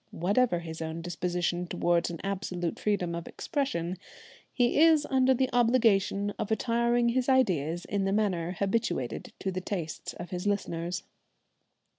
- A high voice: Yes, high, 195 Hz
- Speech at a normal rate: Yes, average, 145 wpm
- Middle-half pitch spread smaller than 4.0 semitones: No, average, 5.3 semitones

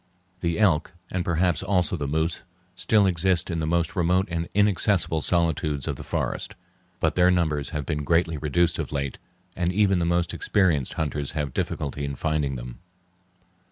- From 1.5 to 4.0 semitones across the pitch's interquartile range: Yes, average, 3.1 semitones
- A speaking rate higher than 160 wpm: Yes, average, 170 wpm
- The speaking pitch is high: No, very low, 85 Hz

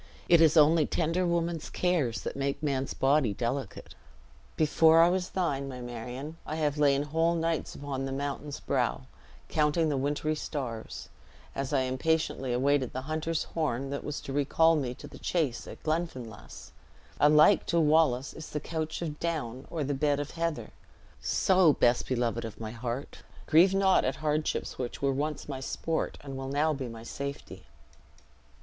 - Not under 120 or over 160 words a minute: No, average, 170 wpm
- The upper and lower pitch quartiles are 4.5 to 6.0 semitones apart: No, average, 3.3 semitones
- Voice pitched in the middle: Yes, medium, 145 Hz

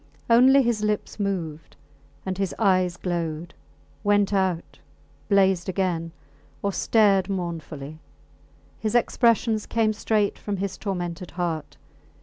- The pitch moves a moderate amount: Yes, average, 3.3 semitones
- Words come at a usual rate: No, slow, 115 wpm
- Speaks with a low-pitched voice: No, high, 190 Hz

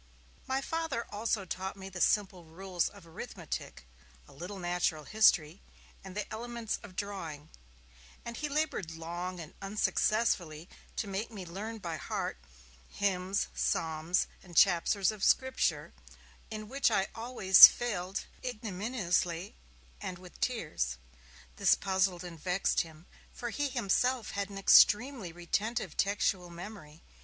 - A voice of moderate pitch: No, high, 195 Hz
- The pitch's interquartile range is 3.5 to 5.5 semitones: Yes, average, 3.9 semitones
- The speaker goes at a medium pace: No, slow, 130 wpm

